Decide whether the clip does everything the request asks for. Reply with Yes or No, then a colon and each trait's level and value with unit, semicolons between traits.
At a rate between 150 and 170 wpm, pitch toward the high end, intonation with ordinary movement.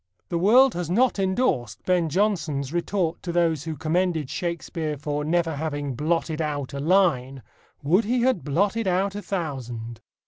No: average, 160 wpm; medium, 165 Hz; average, 4.4 semitones